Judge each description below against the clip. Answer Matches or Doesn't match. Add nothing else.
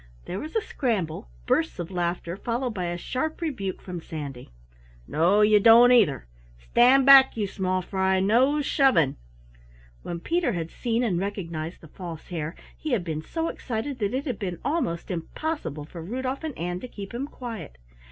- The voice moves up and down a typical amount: Doesn't match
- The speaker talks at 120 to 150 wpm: Doesn't match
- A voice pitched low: Doesn't match